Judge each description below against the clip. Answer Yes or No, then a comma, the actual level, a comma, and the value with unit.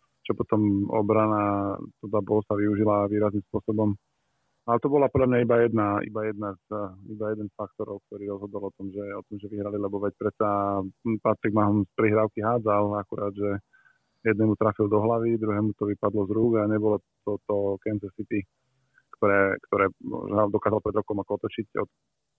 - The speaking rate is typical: No, fast, 180 wpm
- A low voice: Yes, low, 105 Hz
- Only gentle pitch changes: Yes, narrow, 1.1 semitones